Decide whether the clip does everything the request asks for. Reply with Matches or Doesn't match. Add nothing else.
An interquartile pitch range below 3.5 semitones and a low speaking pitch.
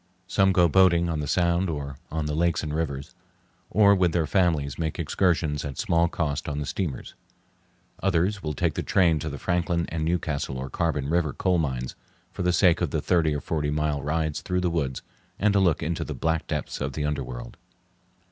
Matches